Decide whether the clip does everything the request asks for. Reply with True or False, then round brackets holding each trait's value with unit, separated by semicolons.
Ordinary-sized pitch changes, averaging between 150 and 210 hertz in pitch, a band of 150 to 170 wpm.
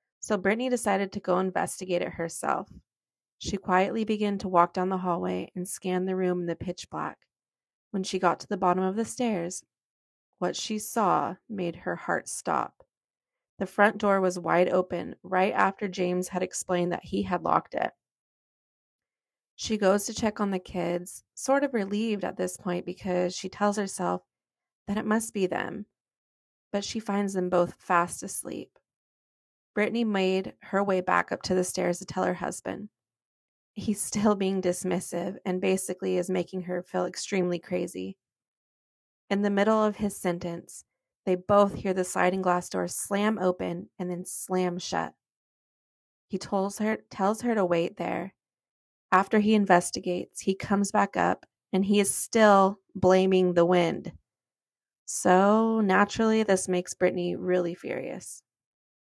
False (2.3 semitones; 185 Hz; 160 wpm)